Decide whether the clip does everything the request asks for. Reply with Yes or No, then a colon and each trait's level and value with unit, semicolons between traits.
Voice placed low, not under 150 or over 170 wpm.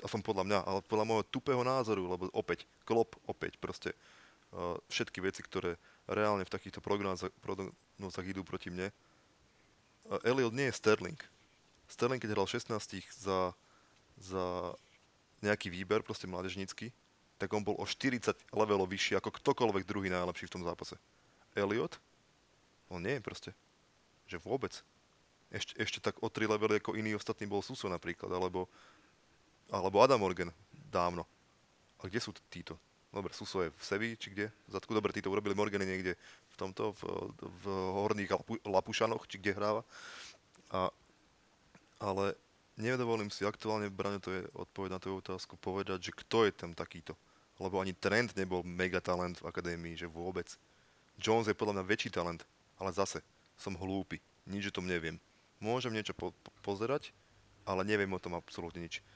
Yes: low, 100 Hz; average, 160 wpm